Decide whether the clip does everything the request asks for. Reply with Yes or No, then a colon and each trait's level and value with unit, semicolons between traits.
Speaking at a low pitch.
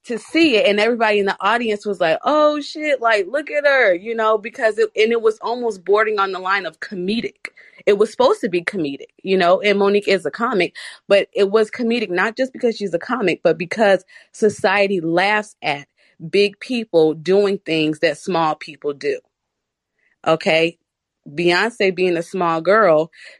No: high, 205 Hz